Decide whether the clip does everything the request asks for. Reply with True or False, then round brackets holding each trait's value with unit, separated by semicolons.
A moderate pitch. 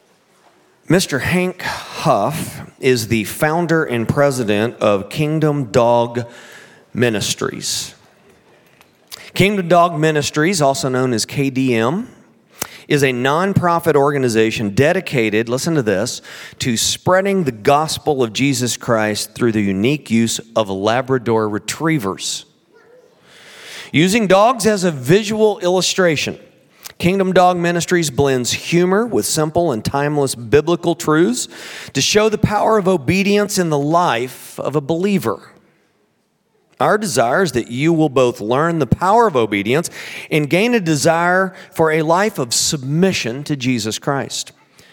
True (150 Hz)